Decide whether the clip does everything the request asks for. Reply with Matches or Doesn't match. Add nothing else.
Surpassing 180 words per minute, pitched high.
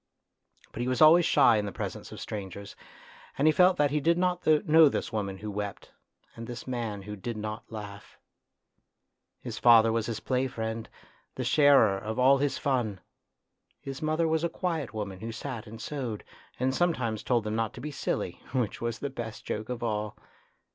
Doesn't match